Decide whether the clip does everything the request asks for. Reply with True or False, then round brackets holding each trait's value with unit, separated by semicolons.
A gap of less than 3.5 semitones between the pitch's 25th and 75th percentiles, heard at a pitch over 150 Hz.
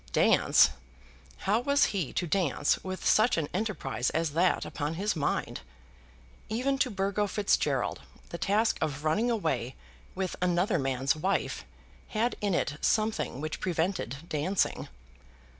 False (5.4 semitones; 185 Hz)